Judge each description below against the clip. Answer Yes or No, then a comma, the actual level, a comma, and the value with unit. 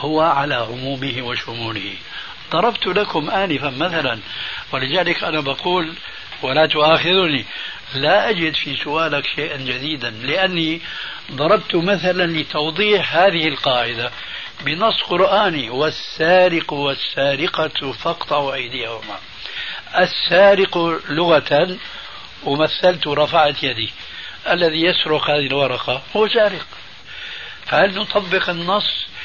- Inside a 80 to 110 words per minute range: Yes, average, 90 wpm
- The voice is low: No, medium, 155 Hz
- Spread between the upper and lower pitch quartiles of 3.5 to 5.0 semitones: Yes, average, 4.7 semitones